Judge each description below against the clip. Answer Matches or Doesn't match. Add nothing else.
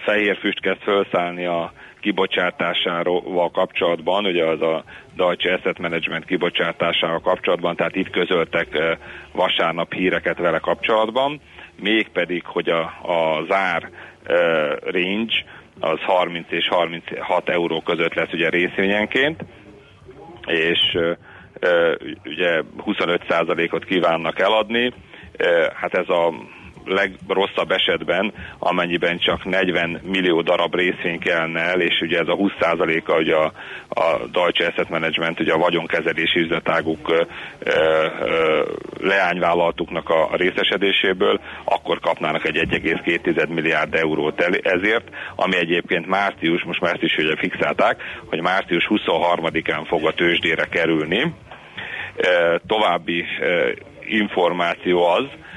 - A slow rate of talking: Doesn't match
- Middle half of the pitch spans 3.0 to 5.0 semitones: Doesn't match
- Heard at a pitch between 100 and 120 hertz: Doesn't match